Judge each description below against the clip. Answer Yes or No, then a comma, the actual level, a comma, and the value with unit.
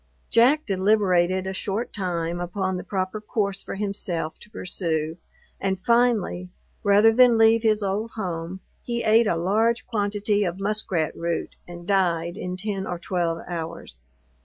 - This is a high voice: Yes, high, 195 Hz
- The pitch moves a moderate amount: Yes, average, 3.5 semitones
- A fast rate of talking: No, average, 150 wpm